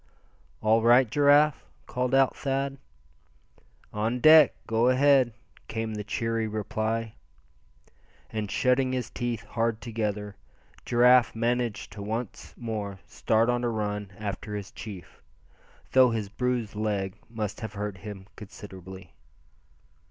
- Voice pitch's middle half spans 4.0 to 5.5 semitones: No, average, 3.0 semitones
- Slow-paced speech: Yes, slow, 120 wpm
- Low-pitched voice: Yes, low, 115 Hz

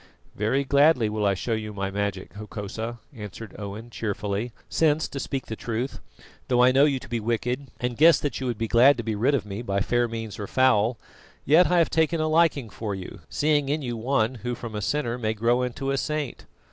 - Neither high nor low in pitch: No, low, 120 Hz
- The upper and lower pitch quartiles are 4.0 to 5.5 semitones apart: Yes, average, 4.3 semitones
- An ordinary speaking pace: No, fast, 220 wpm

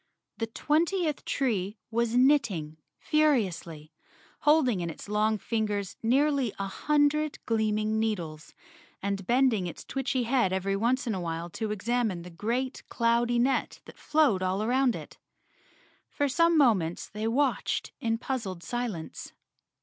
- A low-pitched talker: No, high, 225 Hz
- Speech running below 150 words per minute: Yes, average, 140 wpm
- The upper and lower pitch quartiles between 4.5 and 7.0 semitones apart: Yes, average, 5.1 semitones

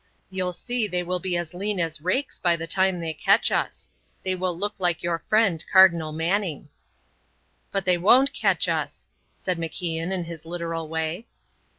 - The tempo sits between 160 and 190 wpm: Yes, average, 175 wpm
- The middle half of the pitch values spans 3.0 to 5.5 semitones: No, narrow, 2.4 semitones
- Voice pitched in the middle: Yes, medium, 180 Hz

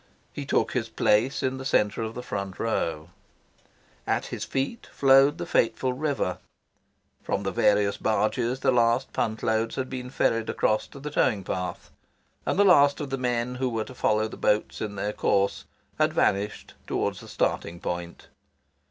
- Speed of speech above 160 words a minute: Yes, average, 175 wpm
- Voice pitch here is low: Yes, low, 115 Hz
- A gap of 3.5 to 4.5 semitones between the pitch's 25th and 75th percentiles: Yes, average, 4.2 semitones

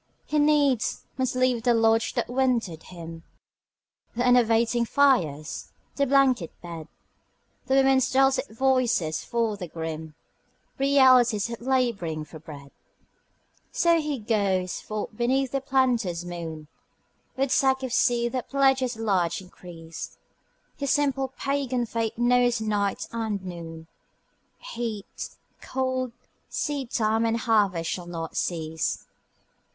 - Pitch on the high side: Yes, high, 230 Hz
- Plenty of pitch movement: Yes, wide, 6.6 semitones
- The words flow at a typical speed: No, slow, 120 wpm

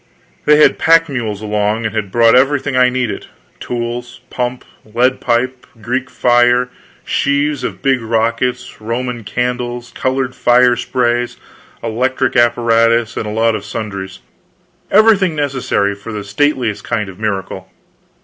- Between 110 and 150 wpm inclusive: Yes, average, 140 wpm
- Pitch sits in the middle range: No, low, 120 Hz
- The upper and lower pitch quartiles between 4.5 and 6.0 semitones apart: No, narrow, 2.5 semitones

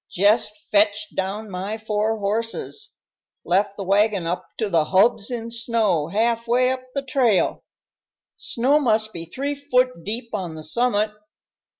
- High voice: Yes, high, 215 Hz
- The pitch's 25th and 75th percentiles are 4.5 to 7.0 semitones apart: No, average, 3.1 semitones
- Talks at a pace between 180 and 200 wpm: No, average, 150 wpm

